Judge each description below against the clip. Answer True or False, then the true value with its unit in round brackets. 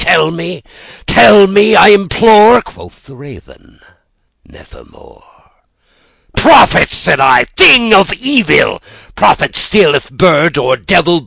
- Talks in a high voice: True (195 Hz)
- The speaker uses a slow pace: True (95 wpm)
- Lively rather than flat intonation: True (5.9 semitones)